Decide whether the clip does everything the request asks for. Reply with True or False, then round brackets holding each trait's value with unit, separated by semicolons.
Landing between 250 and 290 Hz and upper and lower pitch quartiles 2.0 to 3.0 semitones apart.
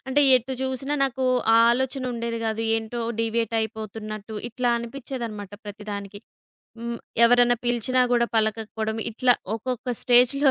False (235 Hz; 2.5 semitones)